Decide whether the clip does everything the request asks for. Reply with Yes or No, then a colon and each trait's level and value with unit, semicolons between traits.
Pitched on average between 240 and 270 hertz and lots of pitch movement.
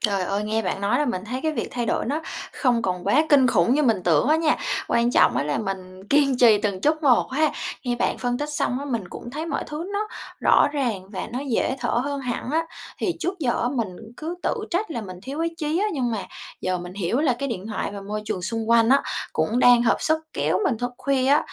Yes: high, 245 Hz; wide, 5.8 semitones